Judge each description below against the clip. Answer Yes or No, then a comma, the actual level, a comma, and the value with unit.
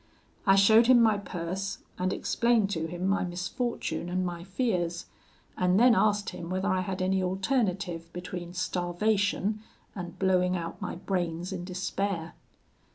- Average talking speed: Yes, average, 150 wpm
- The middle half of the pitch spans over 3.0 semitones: No, narrow, 2.4 semitones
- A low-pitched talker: No, medium, 185 Hz